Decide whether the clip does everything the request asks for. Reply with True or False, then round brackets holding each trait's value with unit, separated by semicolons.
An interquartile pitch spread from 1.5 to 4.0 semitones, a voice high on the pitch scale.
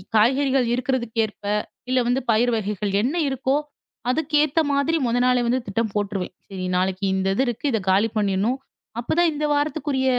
False (4.5 semitones; 245 Hz)